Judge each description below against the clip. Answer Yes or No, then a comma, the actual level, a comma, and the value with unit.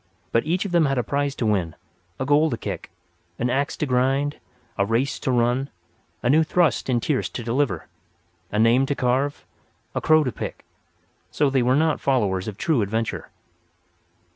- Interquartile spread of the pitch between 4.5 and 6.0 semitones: No, average, 3.7 semitones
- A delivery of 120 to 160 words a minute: No, average, 180 wpm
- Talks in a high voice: No, low, 130 Hz